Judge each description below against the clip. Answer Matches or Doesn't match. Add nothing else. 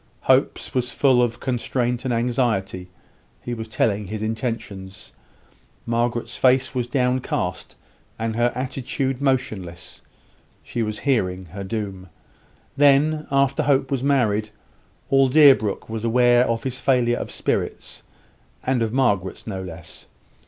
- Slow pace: Matches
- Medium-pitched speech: Doesn't match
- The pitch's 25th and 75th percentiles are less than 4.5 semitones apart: Matches